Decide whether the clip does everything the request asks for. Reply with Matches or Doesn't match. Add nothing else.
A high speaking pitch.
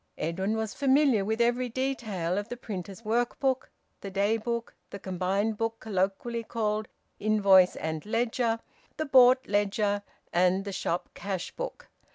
Matches